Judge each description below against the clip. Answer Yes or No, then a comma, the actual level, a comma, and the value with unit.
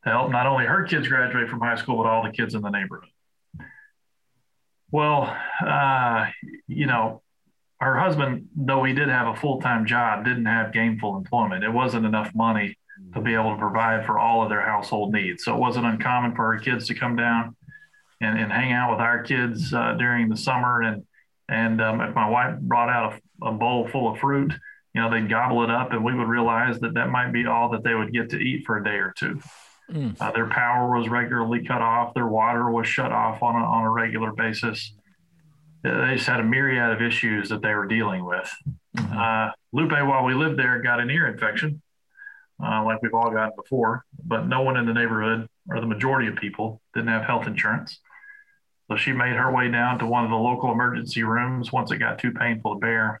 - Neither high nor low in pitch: No, low, 120 Hz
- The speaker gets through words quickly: Yes, fast, 215 wpm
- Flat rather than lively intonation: Yes, narrow, 2.2 semitones